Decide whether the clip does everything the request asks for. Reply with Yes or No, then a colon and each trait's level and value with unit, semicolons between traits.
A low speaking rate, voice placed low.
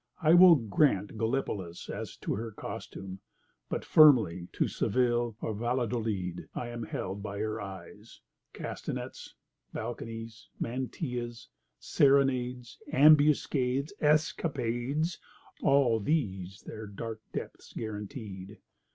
Yes: slow, 100 wpm; low, 120 Hz